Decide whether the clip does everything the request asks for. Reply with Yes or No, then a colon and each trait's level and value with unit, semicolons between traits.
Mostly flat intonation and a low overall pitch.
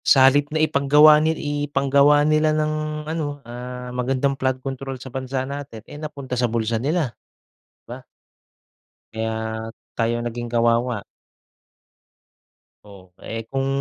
No: average, 3.7 semitones; low, 130 Hz